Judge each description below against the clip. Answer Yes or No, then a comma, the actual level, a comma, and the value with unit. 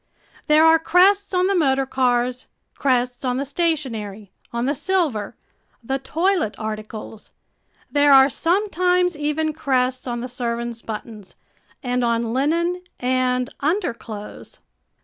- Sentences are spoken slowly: Yes, slow, 125 wpm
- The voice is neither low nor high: No, very high, 265 Hz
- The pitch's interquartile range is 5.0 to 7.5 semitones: Yes, average, 5.3 semitones